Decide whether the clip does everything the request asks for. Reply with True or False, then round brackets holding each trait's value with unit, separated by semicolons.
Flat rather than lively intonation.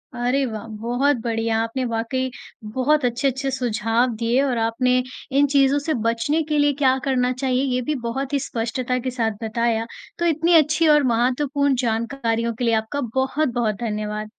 False (3.2 semitones)